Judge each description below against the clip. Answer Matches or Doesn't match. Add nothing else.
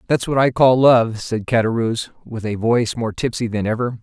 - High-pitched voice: Doesn't match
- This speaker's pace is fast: Matches